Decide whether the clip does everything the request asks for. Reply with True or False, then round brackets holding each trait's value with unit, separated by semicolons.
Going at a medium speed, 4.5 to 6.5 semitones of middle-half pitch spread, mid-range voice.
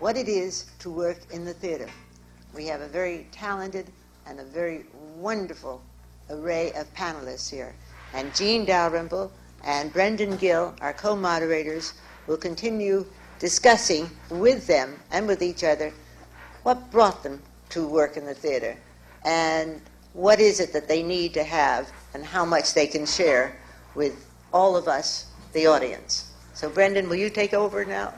True (160 wpm; 5.0 semitones; 165 Hz)